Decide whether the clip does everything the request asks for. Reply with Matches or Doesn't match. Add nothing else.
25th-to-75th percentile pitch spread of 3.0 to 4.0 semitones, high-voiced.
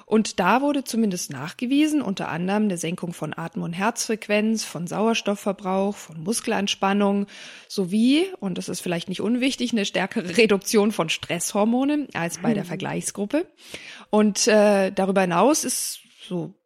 Matches